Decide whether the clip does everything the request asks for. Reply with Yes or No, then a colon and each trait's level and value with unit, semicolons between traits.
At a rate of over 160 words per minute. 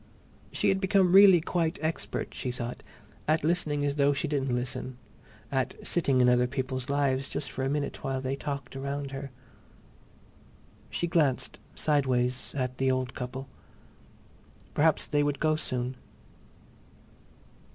No: average, 140 wpm